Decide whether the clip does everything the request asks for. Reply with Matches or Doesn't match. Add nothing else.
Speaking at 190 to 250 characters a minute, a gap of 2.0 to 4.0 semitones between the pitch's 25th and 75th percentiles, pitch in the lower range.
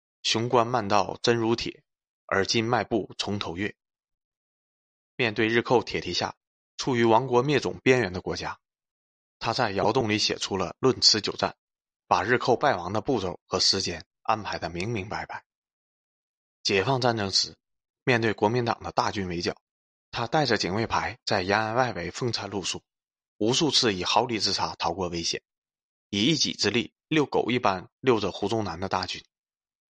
Doesn't match